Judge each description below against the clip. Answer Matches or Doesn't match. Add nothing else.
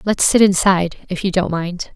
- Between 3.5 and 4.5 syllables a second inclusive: Doesn't match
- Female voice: Matches